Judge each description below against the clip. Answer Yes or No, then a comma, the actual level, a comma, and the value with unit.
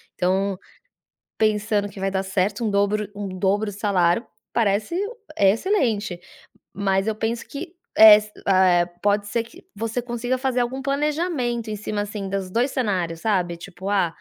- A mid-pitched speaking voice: No, high, 205 Hz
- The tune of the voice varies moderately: Yes, average, 3.2 semitones